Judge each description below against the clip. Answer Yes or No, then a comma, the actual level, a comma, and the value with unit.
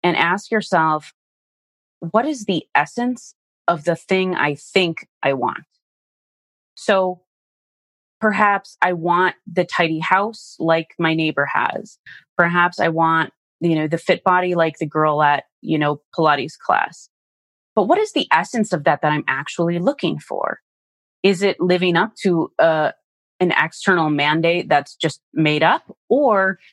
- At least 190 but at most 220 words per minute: No, average, 155 wpm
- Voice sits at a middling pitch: Yes, medium, 170 Hz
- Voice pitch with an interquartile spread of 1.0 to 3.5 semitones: Yes, average, 3.1 semitones